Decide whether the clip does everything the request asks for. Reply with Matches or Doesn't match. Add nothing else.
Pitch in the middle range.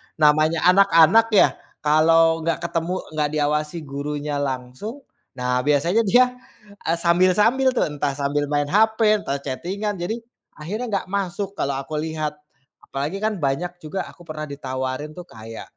Matches